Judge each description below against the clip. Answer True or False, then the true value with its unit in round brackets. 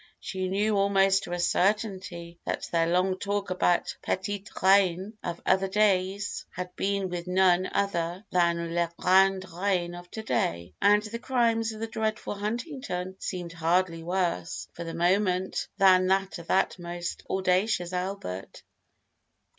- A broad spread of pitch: False (2.4 semitones)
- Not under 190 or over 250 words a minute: False (145 wpm)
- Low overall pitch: False (185 Hz)